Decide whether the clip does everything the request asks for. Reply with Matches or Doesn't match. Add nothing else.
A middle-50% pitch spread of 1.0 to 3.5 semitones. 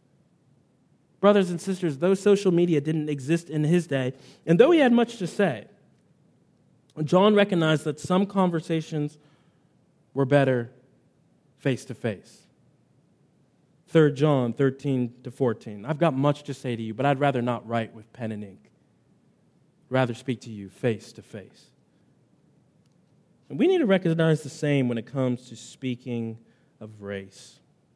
Doesn't match